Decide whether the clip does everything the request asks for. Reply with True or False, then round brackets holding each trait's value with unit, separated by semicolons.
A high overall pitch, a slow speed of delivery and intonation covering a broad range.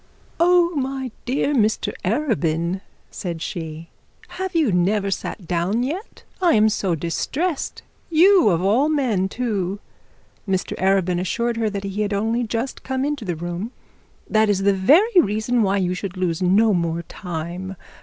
False (205 Hz; 155 wpm; 6.1 semitones)